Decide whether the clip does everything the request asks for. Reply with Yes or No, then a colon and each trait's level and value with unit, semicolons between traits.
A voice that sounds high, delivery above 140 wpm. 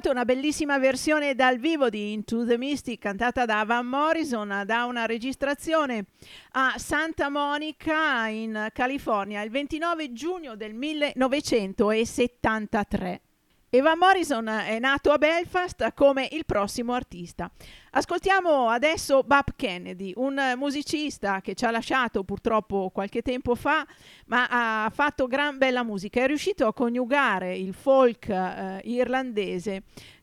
No: very high, 250 Hz; average, 125 wpm